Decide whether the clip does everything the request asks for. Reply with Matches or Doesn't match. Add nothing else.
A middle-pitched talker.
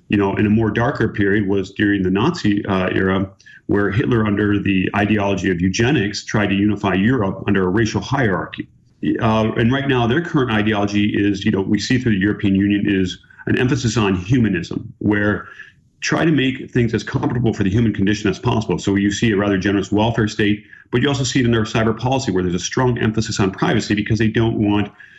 Doesn't match